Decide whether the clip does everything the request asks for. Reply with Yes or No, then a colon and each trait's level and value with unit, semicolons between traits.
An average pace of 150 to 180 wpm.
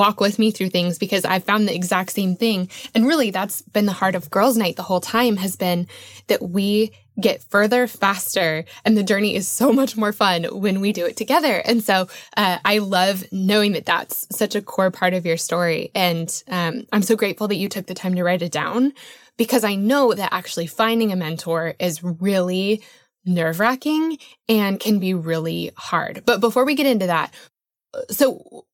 No: average, 200 wpm